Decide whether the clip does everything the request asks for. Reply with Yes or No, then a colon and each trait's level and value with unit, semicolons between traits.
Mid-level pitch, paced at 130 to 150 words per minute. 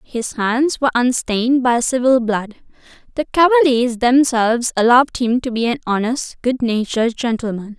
No: high, 245 Hz; average, 140 wpm